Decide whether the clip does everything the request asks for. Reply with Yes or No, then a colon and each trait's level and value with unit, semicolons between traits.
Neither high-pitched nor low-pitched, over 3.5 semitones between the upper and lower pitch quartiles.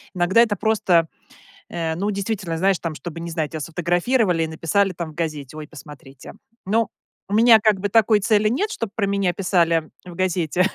Yes: medium, 180 Hz; average, 4.0 semitones